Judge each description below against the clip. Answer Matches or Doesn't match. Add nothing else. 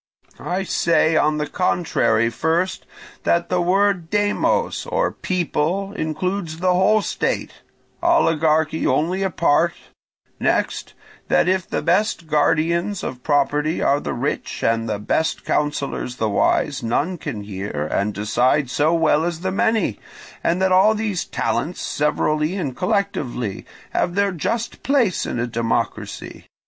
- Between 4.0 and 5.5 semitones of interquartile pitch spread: Matches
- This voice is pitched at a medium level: Matches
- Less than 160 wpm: Matches